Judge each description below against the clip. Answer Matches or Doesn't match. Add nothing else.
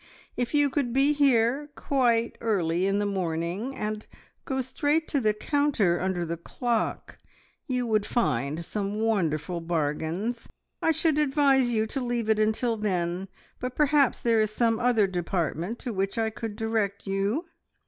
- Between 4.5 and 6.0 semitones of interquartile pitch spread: Matches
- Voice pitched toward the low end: Doesn't match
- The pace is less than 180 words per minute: Matches